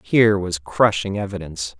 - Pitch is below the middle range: Yes, very low, 95 Hz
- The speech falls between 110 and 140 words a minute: Yes, slow, 135 wpm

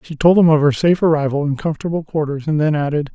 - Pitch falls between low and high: Yes, medium, 150 Hz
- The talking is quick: Yes, fast, 250 wpm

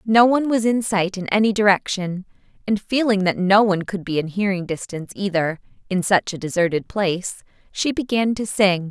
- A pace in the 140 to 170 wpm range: No, average, 190 wpm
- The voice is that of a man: No, female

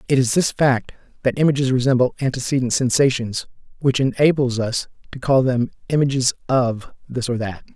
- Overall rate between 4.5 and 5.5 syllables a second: Yes, 5.4 syllables/s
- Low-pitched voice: Yes, low, 130 Hz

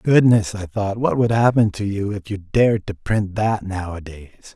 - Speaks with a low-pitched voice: Yes, low, 105 Hz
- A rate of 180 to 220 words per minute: Yes, average, 200 wpm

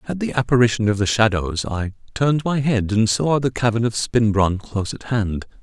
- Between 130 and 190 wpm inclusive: No, fast, 205 wpm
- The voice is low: Yes, low, 115 Hz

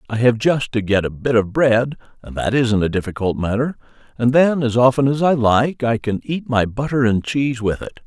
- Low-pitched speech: Yes, low, 120 Hz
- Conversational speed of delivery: No, fast, 230 wpm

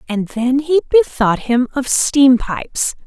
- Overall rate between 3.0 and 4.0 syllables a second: Yes, 3.8 syllables/s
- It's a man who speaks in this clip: No, female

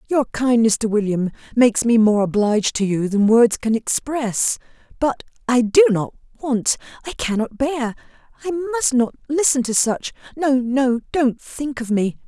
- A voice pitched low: No, high, 245 Hz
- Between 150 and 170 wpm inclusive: Yes, average, 160 wpm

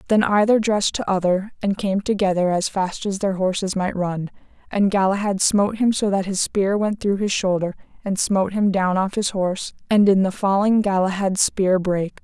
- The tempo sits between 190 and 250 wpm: Yes, average, 200 wpm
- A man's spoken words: No, female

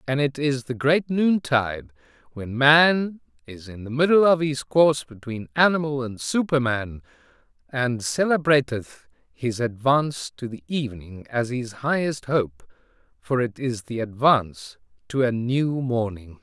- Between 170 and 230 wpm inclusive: No, average, 140 wpm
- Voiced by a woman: No, male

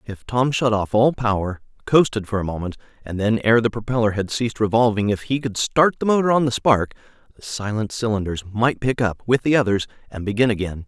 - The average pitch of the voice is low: Yes, low, 110 Hz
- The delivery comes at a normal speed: No, fast, 215 wpm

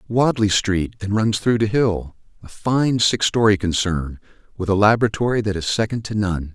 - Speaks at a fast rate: No, average, 175 wpm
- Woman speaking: No, male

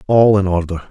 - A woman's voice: No, male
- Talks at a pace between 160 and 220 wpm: Yes, average, 200 wpm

